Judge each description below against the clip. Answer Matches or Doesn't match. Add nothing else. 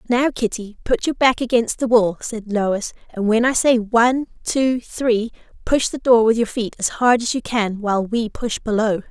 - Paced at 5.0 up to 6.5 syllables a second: Doesn't match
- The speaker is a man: Doesn't match